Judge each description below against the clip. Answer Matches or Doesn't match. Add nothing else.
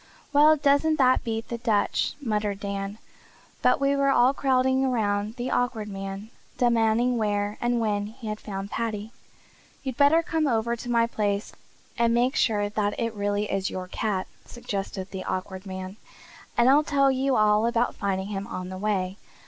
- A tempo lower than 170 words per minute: Doesn't match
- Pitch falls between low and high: Doesn't match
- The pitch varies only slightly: Doesn't match